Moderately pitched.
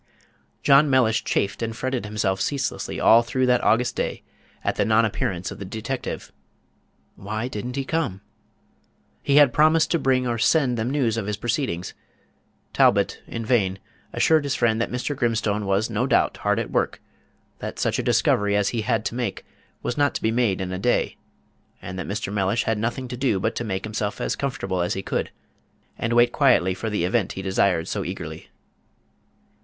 No: low, 115 Hz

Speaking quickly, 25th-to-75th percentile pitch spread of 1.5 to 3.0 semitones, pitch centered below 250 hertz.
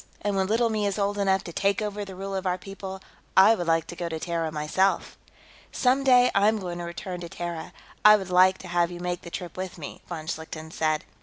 Yes: fast, 245 wpm; narrow, 2.6 semitones; medium, 185 Hz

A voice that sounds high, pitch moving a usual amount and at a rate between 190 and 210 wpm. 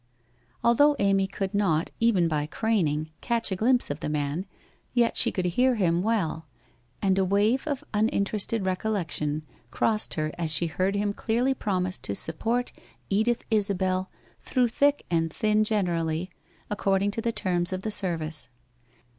No: high, 195 Hz; average, 4.7 semitones; average, 155 wpm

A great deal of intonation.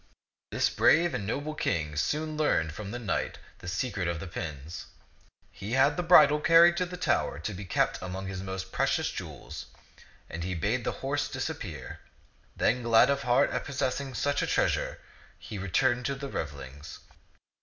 Yes: wide, 8.1 semitones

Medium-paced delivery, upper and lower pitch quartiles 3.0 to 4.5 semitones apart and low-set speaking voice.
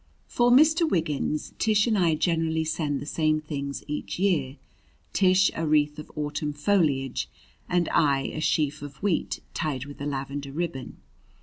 No: average, 160 wpm; average, 3.4 semitones; medium, 155 Hz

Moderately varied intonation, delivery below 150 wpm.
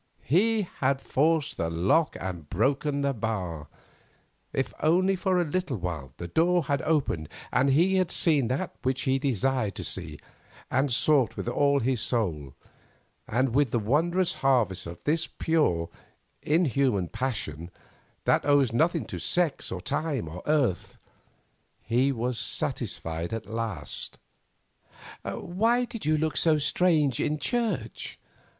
No: wide, 6.4 semitones; average, 140 wpm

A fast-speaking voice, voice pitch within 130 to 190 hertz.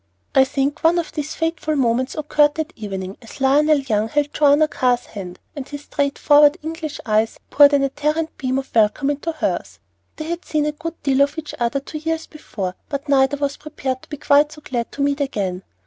No: fast, 210 wpm; very high, 285 Hz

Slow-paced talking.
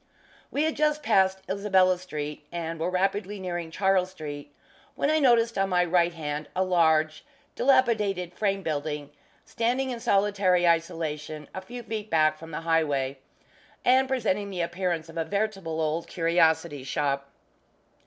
No: average, 150 wpm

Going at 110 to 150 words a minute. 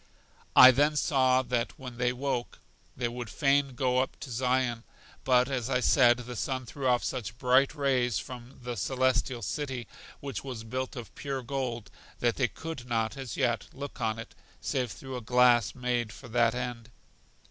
No: average, 180 wpm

